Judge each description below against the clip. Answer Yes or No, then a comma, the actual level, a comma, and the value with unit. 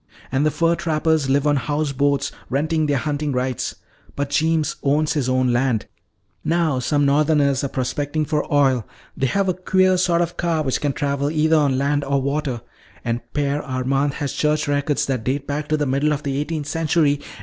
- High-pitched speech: No, medium, 145 Hz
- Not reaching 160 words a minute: No, average, 195 wpm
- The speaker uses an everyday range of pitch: No, narrow, 2.1 semitones